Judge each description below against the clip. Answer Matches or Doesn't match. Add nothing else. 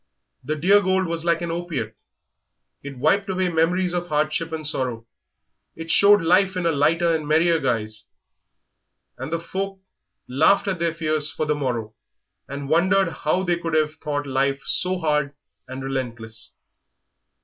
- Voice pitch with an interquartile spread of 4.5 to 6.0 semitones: Doesn't match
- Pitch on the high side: Doesn't match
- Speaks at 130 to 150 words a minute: Doesn't match